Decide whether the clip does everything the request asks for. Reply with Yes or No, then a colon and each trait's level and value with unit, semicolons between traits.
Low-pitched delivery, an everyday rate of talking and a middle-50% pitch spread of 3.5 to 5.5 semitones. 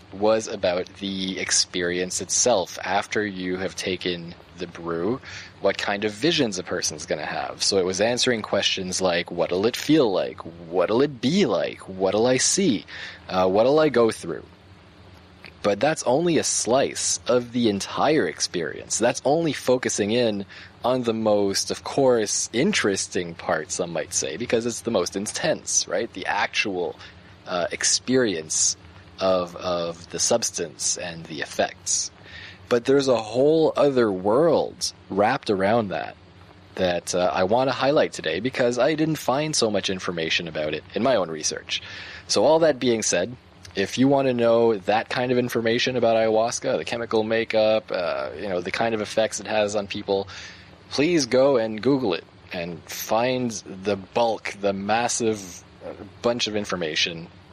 Yes: low, 100 Hz; average, 160 wpm; average, 4.2 semitones